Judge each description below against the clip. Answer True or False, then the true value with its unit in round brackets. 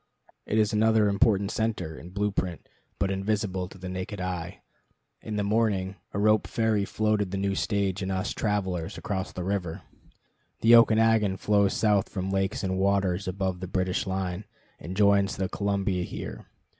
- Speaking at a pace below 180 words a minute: True (170 wpm)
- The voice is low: True (100 Hz)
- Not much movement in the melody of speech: True (1.9 semitones)